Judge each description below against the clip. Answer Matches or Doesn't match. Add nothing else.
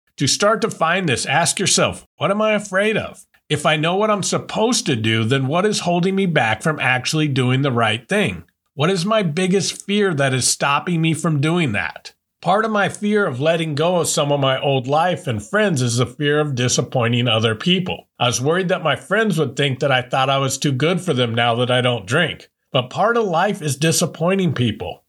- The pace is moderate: Doesn't match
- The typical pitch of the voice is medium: Matches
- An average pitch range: Doesn't match